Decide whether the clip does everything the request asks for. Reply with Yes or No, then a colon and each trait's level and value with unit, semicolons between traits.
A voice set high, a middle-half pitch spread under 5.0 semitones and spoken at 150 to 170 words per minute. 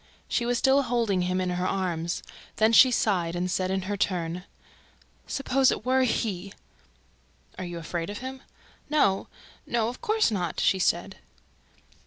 No: high, 195 Hz; average, 5.3 semitones; average, 160 wpm